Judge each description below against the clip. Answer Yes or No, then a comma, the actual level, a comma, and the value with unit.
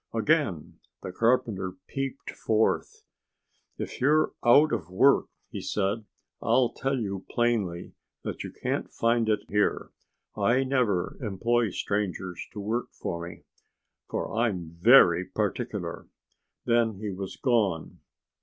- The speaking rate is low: Yes, slow, 125 wpm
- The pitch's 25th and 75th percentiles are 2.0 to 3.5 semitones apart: No, average, 4.2 semitones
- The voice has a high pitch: No, low, 110 Hz